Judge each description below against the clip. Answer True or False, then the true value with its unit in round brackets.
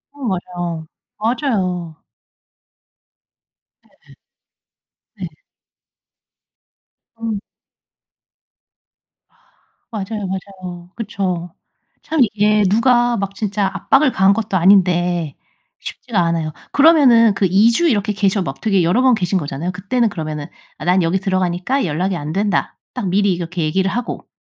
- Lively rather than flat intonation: False (3.8 semitones)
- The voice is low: False (195 Hz)